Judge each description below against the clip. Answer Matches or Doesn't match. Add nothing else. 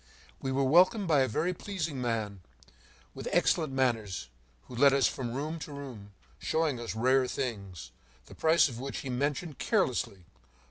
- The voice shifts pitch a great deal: Doesn't match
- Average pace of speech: Matches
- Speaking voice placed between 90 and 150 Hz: Matches